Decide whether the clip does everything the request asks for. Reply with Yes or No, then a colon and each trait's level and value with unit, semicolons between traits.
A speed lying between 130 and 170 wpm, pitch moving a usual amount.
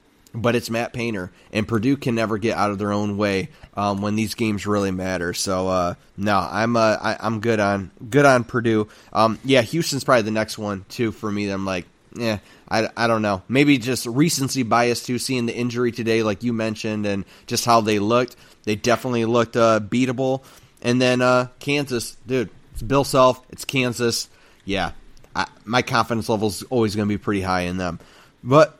No: average, 200 wpm; average, 3.1 semitones